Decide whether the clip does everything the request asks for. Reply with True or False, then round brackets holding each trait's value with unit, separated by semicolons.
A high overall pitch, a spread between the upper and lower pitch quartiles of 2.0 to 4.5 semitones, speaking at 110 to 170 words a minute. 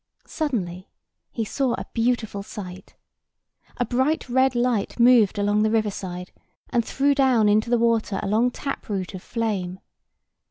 True (225 Hz; 3.6 semitones; 155 wpm)